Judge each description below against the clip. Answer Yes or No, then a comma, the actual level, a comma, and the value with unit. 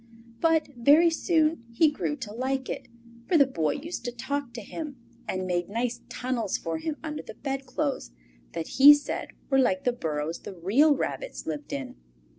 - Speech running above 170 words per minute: Yes, average, 180 wpm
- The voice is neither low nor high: No, very high, 260 Hz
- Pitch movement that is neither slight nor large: No, wide, 7.1 semitones